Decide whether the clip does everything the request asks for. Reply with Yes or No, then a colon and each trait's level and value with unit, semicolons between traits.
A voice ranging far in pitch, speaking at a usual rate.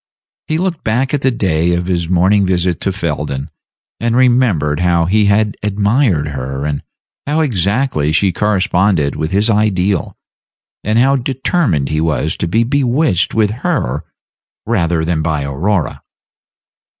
Yes: wide, 6.3 semitones; average, 150 wpm